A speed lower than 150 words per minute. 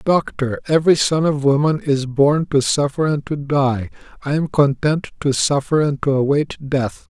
No: average, 175 wpm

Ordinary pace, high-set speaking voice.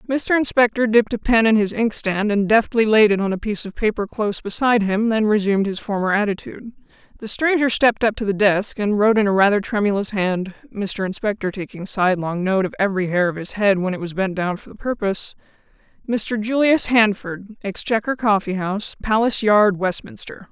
Yes: average, 190 wpm; high, 210 Hz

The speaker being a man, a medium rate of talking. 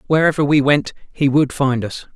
Yes: male; average, 195 wpm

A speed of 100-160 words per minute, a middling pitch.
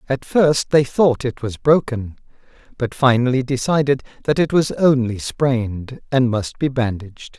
No: average, 155 wpm; low, 130 Hz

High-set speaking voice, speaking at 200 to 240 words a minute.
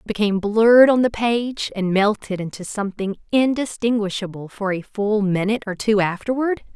No: high, 210 Hz; average, 150 wpm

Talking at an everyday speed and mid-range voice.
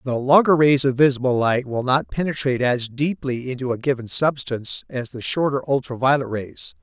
No: average, 185 wpm; low, 130 Hz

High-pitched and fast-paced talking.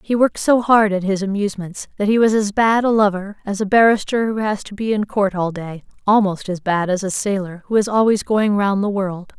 Yes: high, 205 Hz; fast, 235 wpm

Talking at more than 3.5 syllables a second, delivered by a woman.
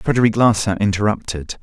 No: 5.7 syllables/s; male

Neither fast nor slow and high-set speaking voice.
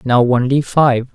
No: average, 155 wpm; low, 130 Hz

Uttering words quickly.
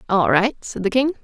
Yes: fast, 245 wpm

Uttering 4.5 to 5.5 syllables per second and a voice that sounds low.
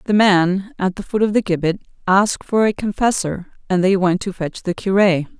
No: 4.8 syllables/s; high, 190 Hz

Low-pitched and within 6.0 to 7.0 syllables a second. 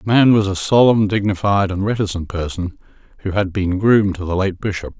No: low, 100 Hz; 5.4 syllables/s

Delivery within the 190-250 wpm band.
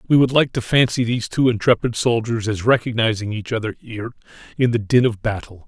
Yes: average, 200 wpm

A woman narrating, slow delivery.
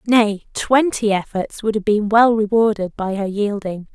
No: female; average, 165 wpm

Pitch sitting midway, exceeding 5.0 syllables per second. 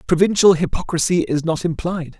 Yes: medium, 165 Hz; 5.4 syllables/s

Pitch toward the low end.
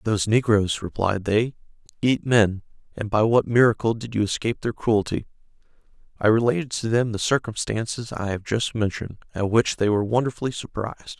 Yes: low, 110 Hz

